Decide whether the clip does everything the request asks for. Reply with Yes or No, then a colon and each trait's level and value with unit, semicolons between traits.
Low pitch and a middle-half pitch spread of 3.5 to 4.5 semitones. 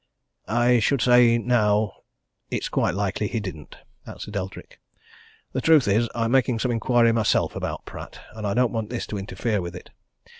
No: low, 115 Hz; average, 2.9 semitones